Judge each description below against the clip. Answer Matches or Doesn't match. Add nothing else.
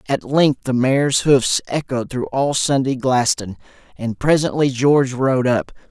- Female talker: Doesn't match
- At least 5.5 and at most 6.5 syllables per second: Doesn't match